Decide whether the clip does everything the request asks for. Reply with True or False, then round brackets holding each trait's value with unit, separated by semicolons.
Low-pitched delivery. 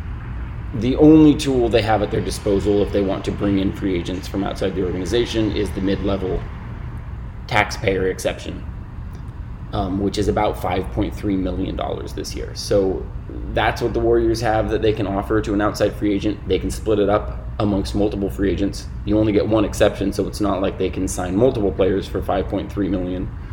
True (100 Hz)